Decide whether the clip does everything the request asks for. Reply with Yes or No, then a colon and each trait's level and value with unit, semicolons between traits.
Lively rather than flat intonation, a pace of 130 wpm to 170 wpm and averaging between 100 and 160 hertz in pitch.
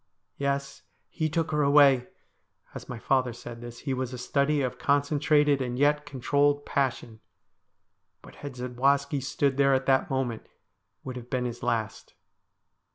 No: narrow, 2.4 semitones; average, 160 wpm; low, 135 Hz